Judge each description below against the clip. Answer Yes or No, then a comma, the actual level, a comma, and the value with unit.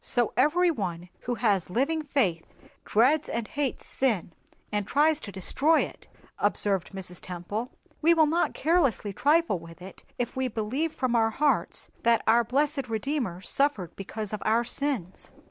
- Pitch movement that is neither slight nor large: No, wide, 6.6 semitones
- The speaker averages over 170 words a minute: No, average, 160 wpm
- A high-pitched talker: Yes, high, 235 Hz